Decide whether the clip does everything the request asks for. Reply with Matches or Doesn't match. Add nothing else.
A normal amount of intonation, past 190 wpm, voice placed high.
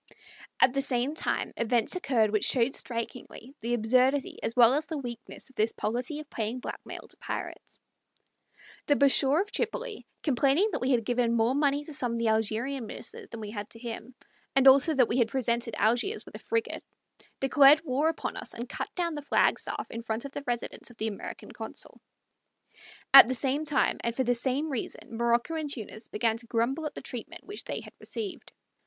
Matches